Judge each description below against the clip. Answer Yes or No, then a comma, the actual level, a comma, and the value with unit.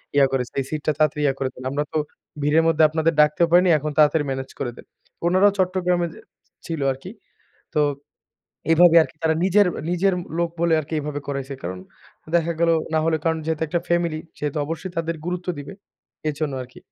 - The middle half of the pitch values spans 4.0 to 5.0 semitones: No, average, 2.7 semitones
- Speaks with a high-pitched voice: No, medium, 160 Hz